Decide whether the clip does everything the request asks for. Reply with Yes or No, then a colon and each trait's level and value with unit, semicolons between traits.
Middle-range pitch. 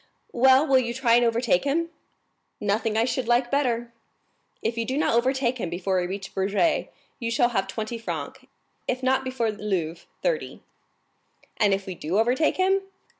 No: high, 235 Hz